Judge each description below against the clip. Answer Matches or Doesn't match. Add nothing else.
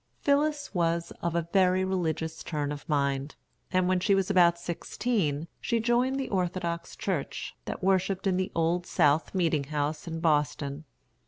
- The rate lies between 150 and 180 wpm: Matches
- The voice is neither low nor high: Matches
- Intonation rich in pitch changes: Doesn't match